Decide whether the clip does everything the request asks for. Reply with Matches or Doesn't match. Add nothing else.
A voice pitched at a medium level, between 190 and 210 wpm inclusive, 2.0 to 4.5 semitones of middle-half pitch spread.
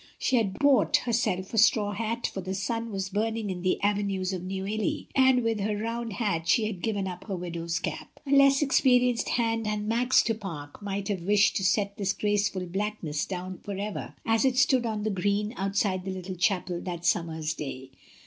Doesn't match